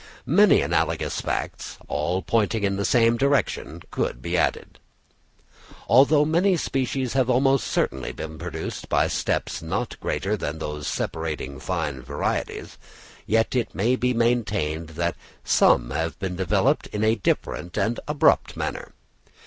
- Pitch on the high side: No, low, 105 Hz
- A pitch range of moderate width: No, wide, 7.4 semitones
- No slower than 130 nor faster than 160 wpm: Yes, average, 140 wpm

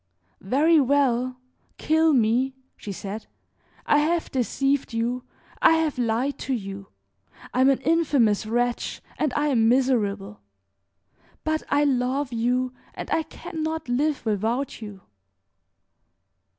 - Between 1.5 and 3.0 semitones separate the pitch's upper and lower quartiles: No, average, 4.2 semitones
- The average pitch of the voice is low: No, very high, 255 Hz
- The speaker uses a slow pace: Yes, slow, 125 wpm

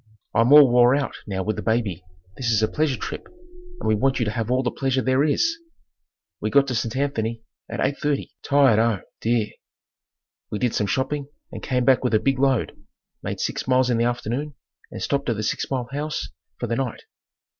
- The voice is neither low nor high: No, low, 125 Hz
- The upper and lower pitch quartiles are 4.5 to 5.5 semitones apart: No, average, 3.3 semitones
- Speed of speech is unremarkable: No, fast, 210 wpm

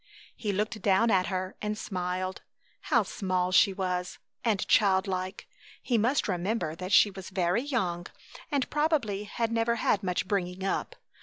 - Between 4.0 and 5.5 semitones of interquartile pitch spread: No, average, 3.2 semitones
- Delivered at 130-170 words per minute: Yes, average, 160 wpm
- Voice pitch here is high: Yes, high, 195 Hz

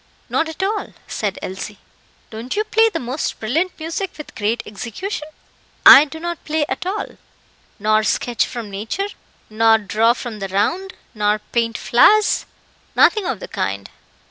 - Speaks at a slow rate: No, average, 155 wpm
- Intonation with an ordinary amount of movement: No, wide, 8.3 semitones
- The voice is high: Yes, high, 240 Hz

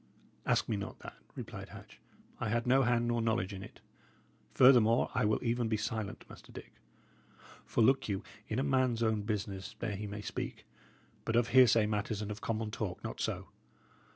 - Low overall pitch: Yes, low, 110 Hz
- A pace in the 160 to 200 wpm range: Yes, average, 185 wpm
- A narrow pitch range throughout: Yes, narrow, 2.1 semitones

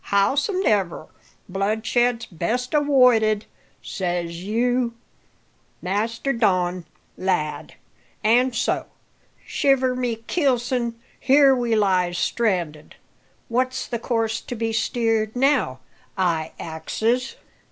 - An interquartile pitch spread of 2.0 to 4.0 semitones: No, average, 4.9 semitones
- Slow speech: Yes, slow, 90 wpm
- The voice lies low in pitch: No, high, 225 Hz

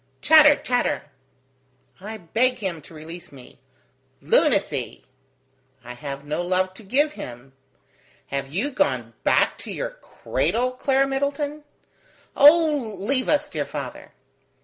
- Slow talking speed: Yes, slow, 125 wpm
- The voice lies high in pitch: Yes, high, 220 Hz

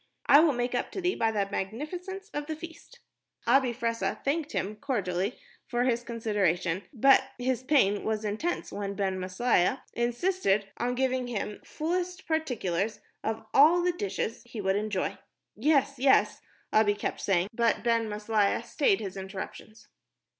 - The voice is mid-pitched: No, high, 235 Hz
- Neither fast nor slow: Yes, average, 155 wpm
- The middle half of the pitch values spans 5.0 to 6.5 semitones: Yes, wide, 5.4 semitones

